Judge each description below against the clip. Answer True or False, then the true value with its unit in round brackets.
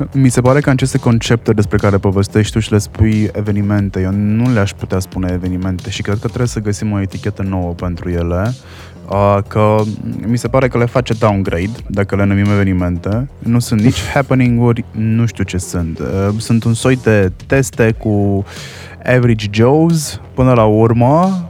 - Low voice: True (105 Hz)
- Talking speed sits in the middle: False (175 wpm)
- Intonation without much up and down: False (3.5 semitones)